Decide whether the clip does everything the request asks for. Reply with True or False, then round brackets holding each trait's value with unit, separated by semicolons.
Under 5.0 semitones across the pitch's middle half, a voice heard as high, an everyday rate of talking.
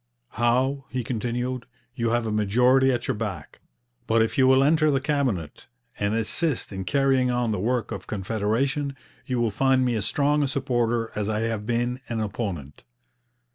False (3.4 semitones; 120 Hz; 175 wpm)